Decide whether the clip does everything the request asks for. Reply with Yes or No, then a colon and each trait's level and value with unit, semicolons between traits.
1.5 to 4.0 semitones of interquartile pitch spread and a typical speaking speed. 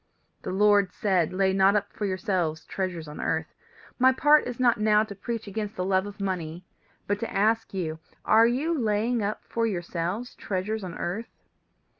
Yes: average, 3.2 semitones; average, 180 wpm